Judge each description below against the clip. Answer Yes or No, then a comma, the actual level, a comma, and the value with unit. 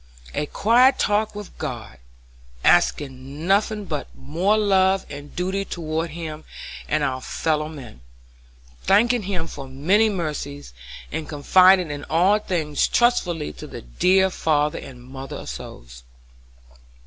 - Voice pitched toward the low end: No, medium, 160 Hz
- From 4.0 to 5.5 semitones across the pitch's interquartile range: Yes, average, 5.1 semitones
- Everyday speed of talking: No, slow, 125 wpm